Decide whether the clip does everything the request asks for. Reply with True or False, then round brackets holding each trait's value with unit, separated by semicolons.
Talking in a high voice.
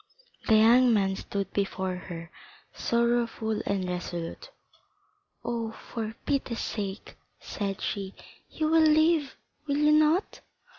True (220 Hz)